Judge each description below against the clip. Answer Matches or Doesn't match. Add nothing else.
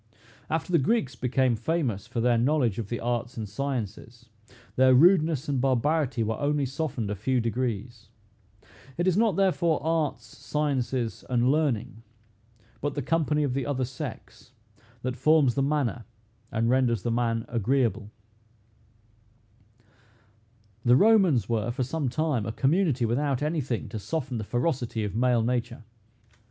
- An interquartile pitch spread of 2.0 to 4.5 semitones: Matches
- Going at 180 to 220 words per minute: Doesn't match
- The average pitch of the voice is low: Matches